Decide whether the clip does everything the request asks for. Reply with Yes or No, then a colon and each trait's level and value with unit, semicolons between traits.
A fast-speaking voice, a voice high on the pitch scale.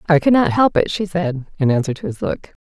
Yes: fast, 275 wpm; high, 225 Hz